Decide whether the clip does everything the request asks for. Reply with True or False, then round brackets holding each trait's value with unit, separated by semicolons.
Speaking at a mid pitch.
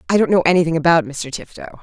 True (165 Hz)